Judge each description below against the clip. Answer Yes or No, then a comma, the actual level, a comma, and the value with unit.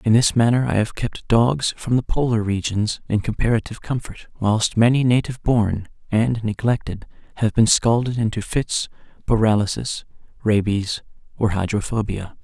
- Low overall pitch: Yes, low, 110 Hz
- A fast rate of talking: No, average, 140 wpm